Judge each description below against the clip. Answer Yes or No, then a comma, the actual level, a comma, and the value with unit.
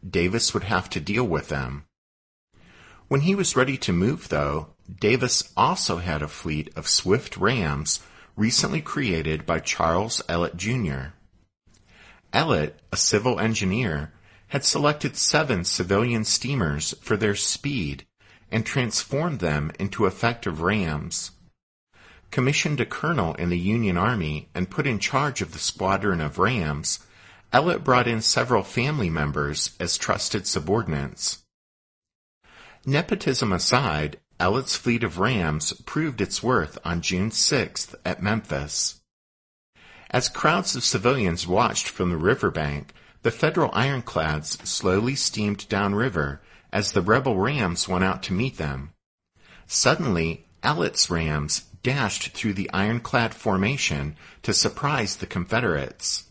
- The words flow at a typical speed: No, slow, 130 wpm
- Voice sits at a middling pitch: No, very low, 95 Hz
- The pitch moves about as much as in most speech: No, wide, 7.0 semitones